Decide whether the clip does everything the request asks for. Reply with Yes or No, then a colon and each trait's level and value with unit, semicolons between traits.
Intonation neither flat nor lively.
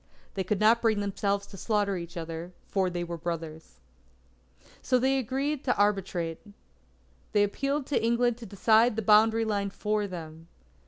Yes: average, 4.3 semitones